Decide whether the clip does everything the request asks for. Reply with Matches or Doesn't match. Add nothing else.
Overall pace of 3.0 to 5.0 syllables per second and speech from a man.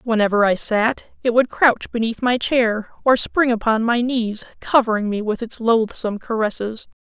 Doesn't match